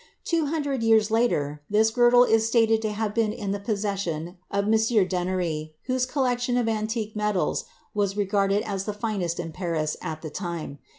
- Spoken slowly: No, average, 180 wpm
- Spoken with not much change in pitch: No, average, 3.5 semitones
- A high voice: Yes, high, 210 Hz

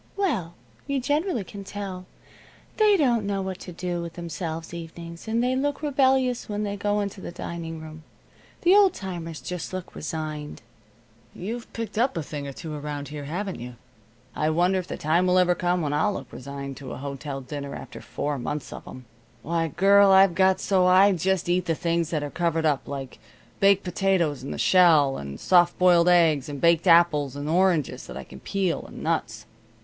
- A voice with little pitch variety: No, average, 4.4 semitones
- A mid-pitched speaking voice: Yes, medium, 175 Hz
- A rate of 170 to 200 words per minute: Yes, average, 195 wpm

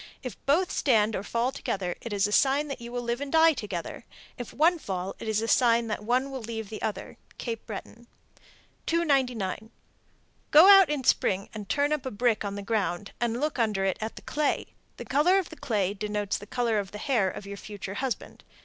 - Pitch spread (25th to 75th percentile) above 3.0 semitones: Yes, average, 5.0 semitones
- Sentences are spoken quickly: Yes, fast, 215 wpm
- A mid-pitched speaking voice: No, high, 230 Hz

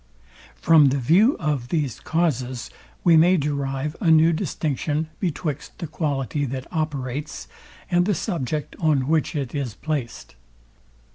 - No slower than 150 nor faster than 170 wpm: No, slow, 135 wpm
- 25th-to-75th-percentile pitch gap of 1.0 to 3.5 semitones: Yes, average, 3.2 semitones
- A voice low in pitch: No, medium, 150 Hz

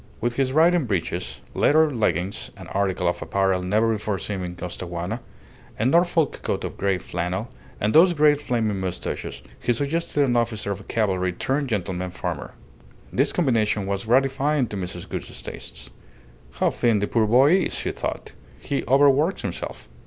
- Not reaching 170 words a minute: Yes, average, 160 wpm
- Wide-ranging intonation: Yes, wide, 6.4 semitones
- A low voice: Yes, low, 110 Hz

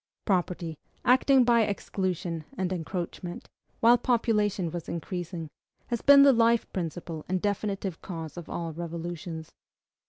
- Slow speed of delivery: Yes, slow, 125 wpm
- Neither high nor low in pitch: Yes, medium, 180 Hz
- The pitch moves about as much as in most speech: Yes, average, 4.6 semitones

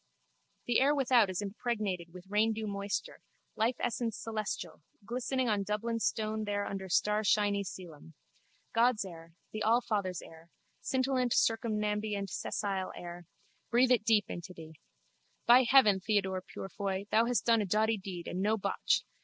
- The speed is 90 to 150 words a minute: Yes, average, 145 wpm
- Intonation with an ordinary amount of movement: Yes, average, 3.1 semitones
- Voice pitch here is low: No, high, 210 Hz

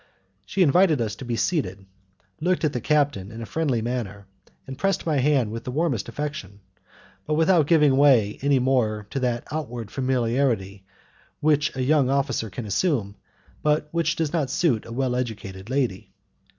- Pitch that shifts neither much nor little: Yes, average, 4.9 semitones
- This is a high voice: No, low, 130 Hz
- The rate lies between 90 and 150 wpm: No, average, 170 wpm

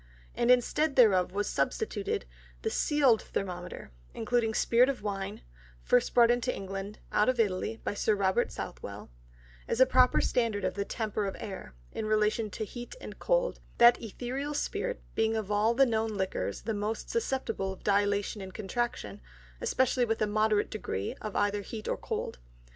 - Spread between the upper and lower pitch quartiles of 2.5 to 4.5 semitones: Yes, average, 3.3 semitones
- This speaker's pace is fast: No, average, 170 wpm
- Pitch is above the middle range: Yes, high, 220 Hz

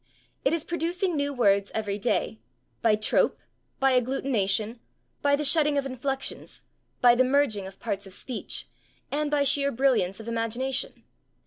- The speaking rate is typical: Yes, average, 150 wpm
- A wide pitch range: No, average, 4.9 semitones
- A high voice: Yes, very high, 255 Hz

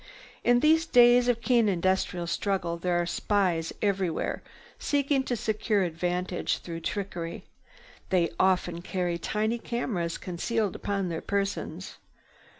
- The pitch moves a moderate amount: Yes, average, 4.7 semitones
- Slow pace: Yes, slow, 125 wpm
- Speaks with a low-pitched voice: No, high, 195 Hz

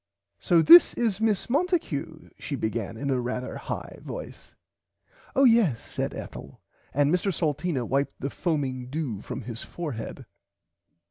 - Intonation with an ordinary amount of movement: No, wide, 6.8 semitones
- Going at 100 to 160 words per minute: Yes, average, 140 wpm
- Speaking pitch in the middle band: Yes, medium, 145 Hz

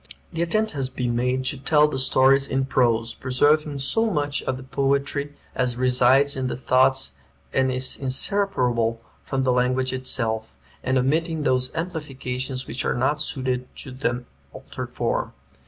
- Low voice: Yes, low, 130 Hz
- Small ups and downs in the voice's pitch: Yes, narrow, 2.2 semitones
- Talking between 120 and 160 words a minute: Yes, average, 155 wpm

